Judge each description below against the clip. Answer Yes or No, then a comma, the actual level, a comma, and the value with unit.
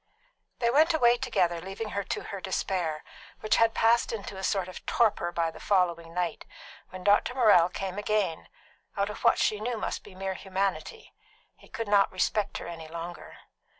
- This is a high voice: Yes, high, 195 Hz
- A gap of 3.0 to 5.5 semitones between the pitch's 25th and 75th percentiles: Yes, average, 3.9 semitones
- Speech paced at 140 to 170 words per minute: No, average, 185 wpm